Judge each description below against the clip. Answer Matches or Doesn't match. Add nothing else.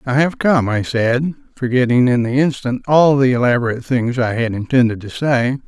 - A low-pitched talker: Matches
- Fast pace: Doesn't match